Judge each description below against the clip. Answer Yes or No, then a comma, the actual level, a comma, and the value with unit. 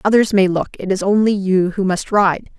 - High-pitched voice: Yes, high, 195 Hz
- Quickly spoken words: Yes, fast, 230 wpm